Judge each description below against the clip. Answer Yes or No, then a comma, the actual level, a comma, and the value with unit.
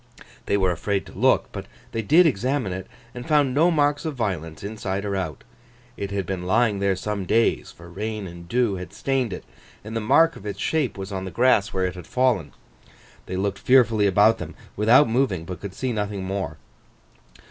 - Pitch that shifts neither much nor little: Yes, average, 4.7 semitones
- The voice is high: No, low, 105 Hz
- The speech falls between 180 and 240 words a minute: Yes, average, 200 wpm